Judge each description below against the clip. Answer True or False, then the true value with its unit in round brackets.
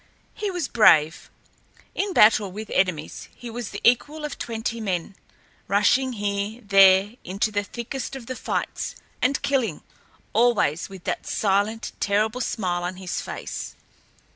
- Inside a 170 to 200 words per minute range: False (140 wpm)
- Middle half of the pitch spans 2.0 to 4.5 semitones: True (4.0 semitones)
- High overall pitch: True (215 Hz)